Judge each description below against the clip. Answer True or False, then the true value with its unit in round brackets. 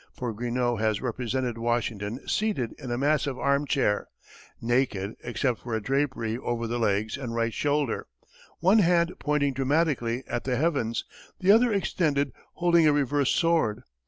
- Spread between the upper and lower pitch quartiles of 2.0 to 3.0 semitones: False (4.1 semitones)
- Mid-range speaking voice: False (130 Hz)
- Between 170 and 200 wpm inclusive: False (150 wpm)